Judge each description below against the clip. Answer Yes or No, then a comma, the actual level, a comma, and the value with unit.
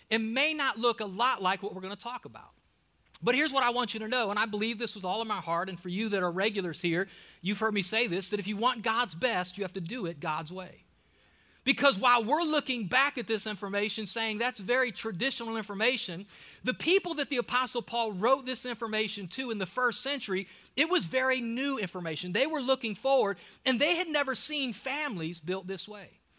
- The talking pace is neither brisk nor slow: No, fast, 225 wpm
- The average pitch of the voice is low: No, high, 225 Hz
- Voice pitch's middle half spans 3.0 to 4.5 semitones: No, average, 4.9 semitones